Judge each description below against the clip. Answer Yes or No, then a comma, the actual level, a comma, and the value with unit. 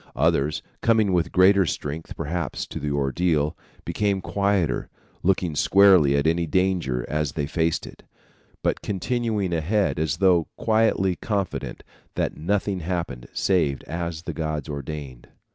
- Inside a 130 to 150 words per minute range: Yes, slow, 135 wpm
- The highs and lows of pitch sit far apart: No, average, 4.3 semitones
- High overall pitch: No, very low, 85 Hz